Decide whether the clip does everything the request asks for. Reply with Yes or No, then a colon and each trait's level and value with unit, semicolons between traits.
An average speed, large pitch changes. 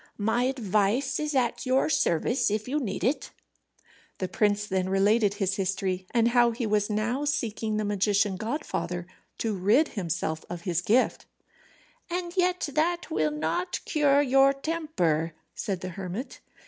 Yes: average, 150 wpm; wide, 6.0 semitones